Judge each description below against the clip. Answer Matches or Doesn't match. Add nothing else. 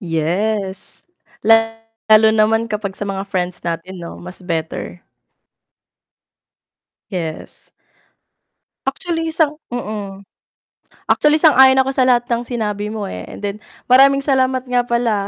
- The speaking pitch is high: Matches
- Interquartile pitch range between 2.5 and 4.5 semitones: Doesn't match